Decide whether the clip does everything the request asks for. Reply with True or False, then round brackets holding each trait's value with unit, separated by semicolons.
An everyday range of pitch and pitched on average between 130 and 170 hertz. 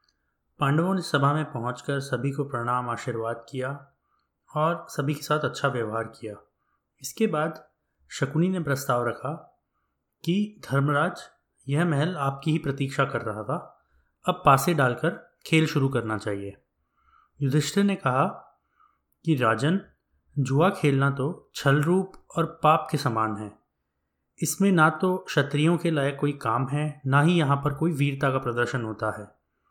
True (4.9 semitones; 140 Hz)